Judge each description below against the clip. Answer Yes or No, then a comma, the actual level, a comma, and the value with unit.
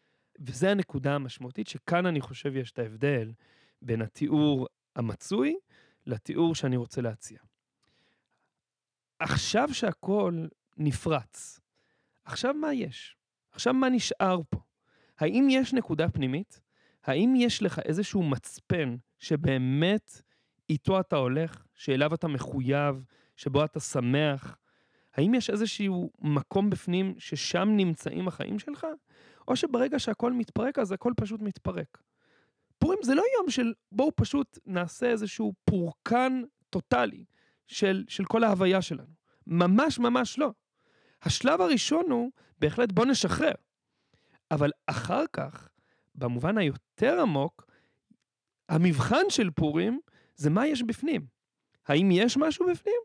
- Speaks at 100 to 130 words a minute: Yes, average, 120 wpm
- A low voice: No, medium, 185 Hz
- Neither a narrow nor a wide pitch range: No, wide, 8.6 semitones